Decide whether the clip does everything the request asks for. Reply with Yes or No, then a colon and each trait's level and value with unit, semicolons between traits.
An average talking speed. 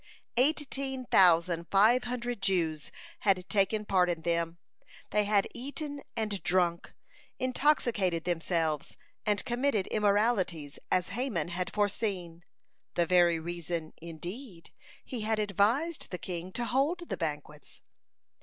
No: slow, 120 wpm